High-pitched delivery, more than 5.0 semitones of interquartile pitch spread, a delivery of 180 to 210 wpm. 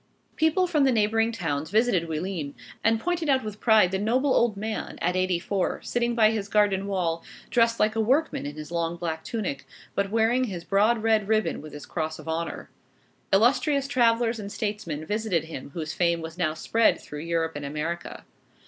Yes: high, 200 Hz; wide, 5.4 semitones; average, 190 wpm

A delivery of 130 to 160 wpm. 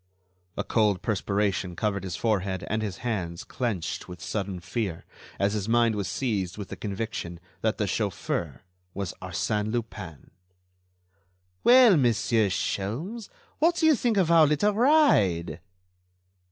Yes: average, 140 wpm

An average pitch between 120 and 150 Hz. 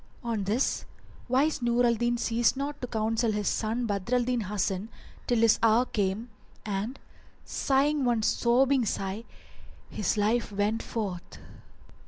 No: high, 230 Hz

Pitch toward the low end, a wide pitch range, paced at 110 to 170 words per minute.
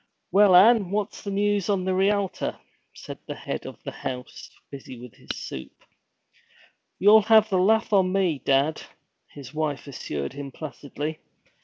No: medium, 185 Hz; wide, 6.2 semitones; average, 155 wpm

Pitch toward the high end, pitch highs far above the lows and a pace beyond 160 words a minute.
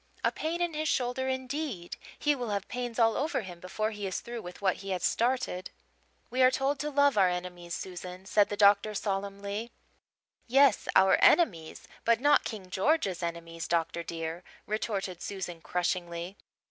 Yes: high, 200 Hz; wide, 6.0 semitones; average, 170 wpm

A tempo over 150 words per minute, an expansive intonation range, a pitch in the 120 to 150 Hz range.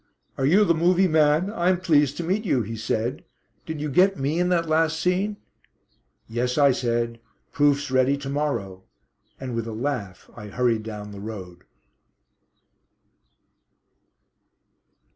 No: average, 145 wpm; wide, 6.2 semitones; medium, 140 Hz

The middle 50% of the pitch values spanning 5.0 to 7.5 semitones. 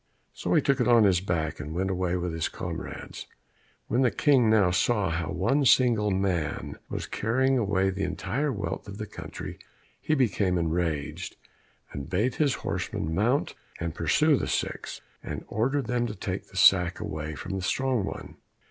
Yes: wide, 5.6 semitones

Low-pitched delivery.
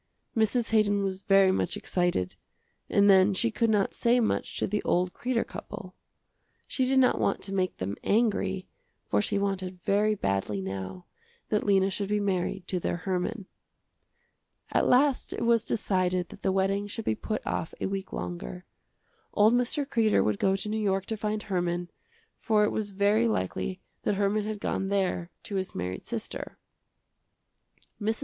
No: high, 195 Hz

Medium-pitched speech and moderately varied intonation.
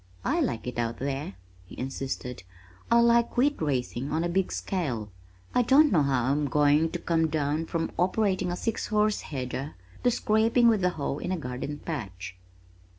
No: medium, 155 Hz; wide, 6.7 semitones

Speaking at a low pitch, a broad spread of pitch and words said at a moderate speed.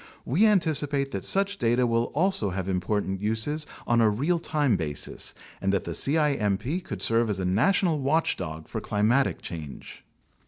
Yes: low, 115 Hz; wide, 7.4 semitones; average, 160 wpm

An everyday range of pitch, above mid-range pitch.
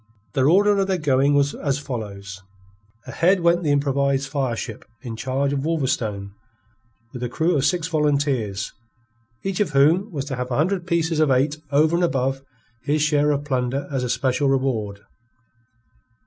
No: average, 3.4 semitones; medium, 140 Hz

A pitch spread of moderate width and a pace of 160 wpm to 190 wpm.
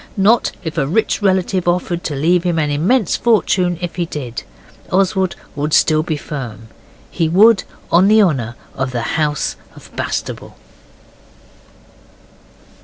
No: average, 4.2 semitones; average, 140 wpm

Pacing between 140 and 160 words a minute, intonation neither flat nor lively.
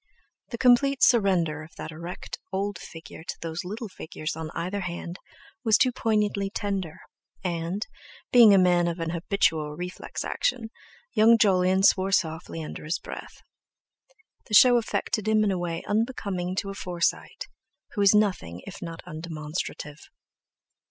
Yes: average, 150 wpm; average, 4.1 semitones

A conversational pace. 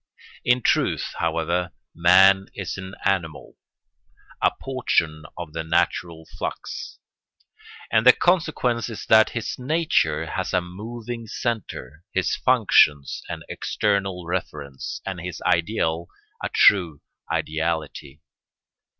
No: slow, 110 wpm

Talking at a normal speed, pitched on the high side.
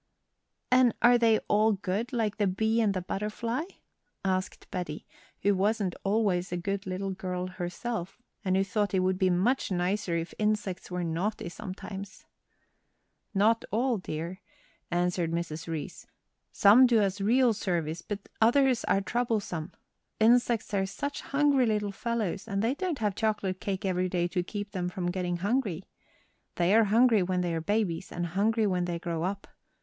Yes: average, 165 wpm; high, 195 Hz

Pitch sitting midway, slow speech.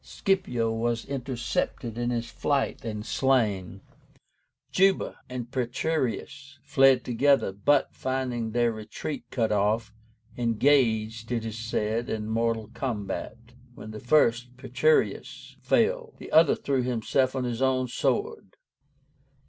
No: low, 120 Hz; slow, 120 wpm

